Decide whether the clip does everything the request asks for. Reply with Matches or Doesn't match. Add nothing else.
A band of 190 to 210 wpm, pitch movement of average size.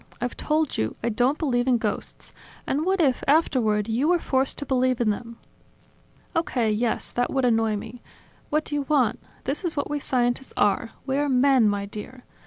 Matches